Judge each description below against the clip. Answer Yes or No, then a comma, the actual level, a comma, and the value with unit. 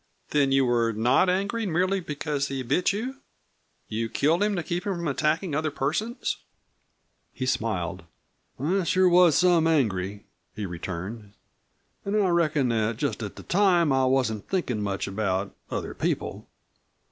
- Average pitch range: No, wide, 8.0 semitones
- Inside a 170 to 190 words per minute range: No, average, 155 wpm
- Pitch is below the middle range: No, medium, 145 Hz